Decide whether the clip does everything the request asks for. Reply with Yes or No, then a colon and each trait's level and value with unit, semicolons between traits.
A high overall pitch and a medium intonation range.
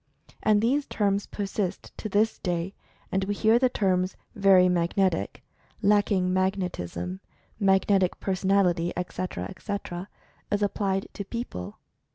No: high, 195 Hz; narrow, 2.1 semitones